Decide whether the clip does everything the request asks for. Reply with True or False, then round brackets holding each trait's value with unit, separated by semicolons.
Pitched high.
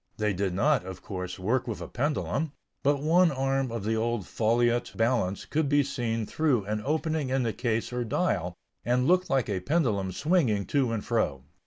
False (120 Hz)